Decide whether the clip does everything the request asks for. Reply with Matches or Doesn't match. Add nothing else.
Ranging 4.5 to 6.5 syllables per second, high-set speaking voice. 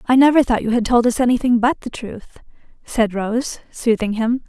Matches